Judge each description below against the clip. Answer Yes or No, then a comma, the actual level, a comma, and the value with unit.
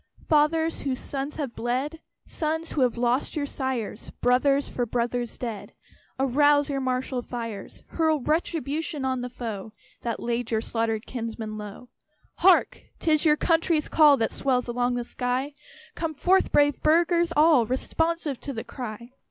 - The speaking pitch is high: Yes, very high, 260 Hz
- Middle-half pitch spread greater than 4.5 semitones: No, average, 4.1 semitones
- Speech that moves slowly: No, average, 155 wpm